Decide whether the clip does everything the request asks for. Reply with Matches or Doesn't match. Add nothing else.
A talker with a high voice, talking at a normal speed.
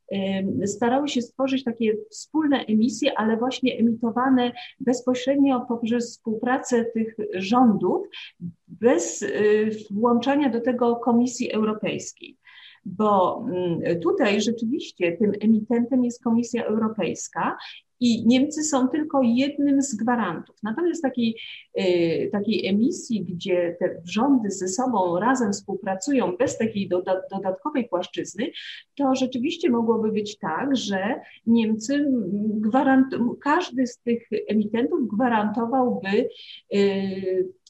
Doesn't match